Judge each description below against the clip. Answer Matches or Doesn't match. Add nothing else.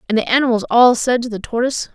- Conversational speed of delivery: Doesn't match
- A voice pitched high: Matches